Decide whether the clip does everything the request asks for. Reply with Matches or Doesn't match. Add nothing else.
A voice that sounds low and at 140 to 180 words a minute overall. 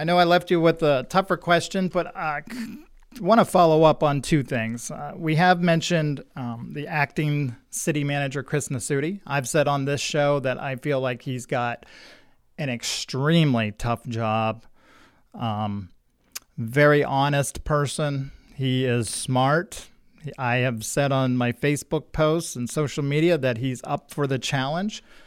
Doesn't match